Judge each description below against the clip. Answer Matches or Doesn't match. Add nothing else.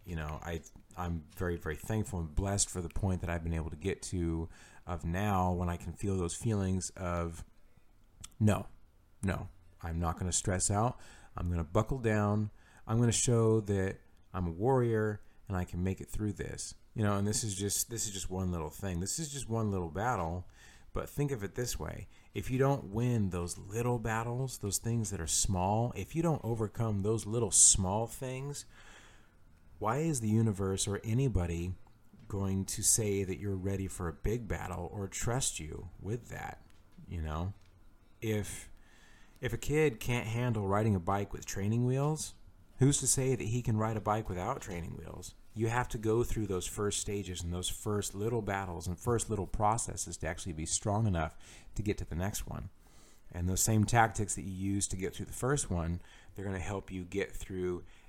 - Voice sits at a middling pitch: Doesn't match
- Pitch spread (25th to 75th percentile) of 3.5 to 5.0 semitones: Matches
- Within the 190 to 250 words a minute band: Matches